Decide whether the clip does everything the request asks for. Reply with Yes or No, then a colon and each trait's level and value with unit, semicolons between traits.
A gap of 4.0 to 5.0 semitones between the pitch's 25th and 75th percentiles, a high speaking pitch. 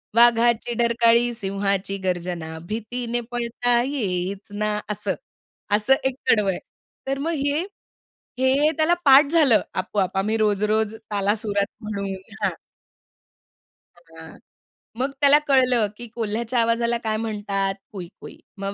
No: average, 3.4 semitones; high, 220 Hz